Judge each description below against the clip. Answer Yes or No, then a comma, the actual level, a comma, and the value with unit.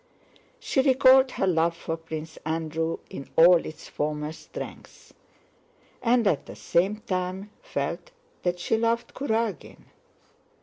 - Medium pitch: Yes, medium, 180 Hz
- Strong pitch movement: Yes, wide, 6.1 semitones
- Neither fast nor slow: No, slow, 125 wpm